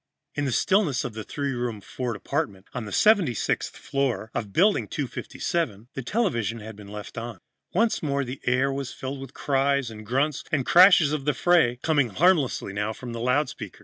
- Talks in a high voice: No, low, 135 Hz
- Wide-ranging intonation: No, average, 4.4 semitones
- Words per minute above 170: Yes, average, 195 wpm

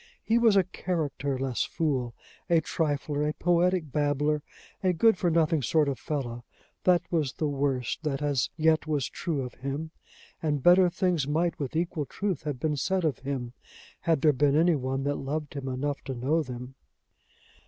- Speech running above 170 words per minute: Yes, average, 180 wpm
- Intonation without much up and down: No, average, 3.4 semitones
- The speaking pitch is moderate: Yes, medium, 150 Hz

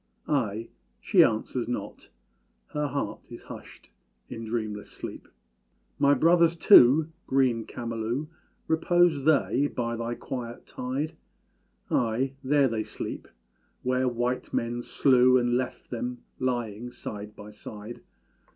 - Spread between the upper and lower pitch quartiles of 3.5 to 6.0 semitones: No, average, 3.1 semitones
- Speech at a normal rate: No, slow, 120 wpm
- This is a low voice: Yes, low, 125 Hz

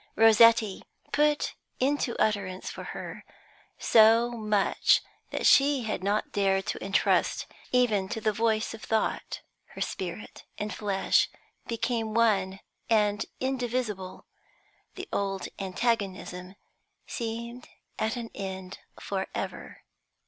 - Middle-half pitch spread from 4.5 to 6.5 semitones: No, average, 3.1 semitones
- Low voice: No, high, 220 Hz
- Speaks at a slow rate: Yes, slow, 110 wpm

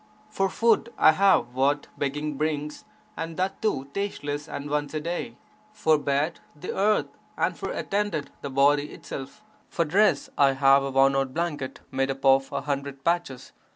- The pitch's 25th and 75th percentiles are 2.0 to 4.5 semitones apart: Yes, average, 4.0 semitones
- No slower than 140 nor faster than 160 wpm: No, average, 170 wpm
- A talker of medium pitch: Yes, medium, 145 Hz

